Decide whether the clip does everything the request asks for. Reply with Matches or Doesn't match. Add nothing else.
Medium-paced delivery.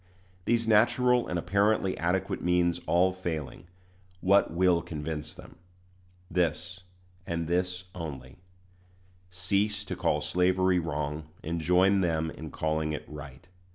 Doesn't match